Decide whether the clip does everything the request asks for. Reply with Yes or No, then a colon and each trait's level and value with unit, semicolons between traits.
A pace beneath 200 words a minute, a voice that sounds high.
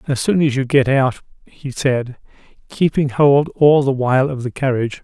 No: average, 190 wpm; low, 135 Hz